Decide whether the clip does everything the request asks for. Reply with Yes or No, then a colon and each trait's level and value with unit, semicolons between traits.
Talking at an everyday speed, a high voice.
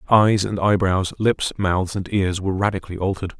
No: average, 175 wpm; very low, 95 Hz